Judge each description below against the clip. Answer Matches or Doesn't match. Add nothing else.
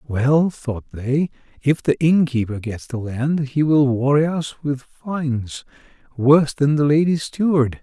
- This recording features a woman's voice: Doesn't match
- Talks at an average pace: Matches